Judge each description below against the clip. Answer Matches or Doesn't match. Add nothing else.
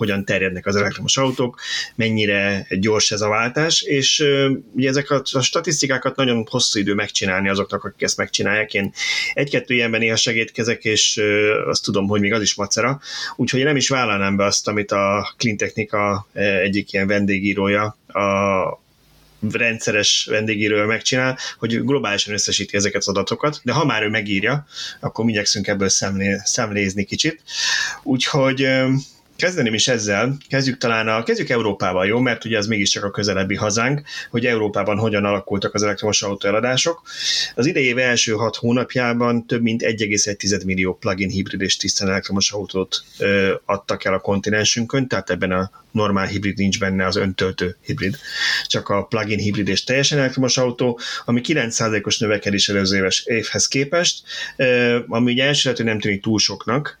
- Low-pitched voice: Matches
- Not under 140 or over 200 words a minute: Matches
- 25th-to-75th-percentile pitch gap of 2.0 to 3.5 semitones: Doesn't match